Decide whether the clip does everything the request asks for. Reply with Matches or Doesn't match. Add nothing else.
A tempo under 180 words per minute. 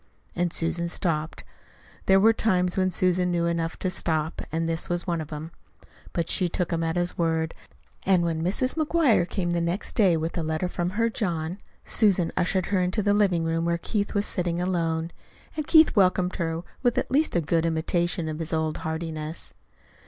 Doesn't match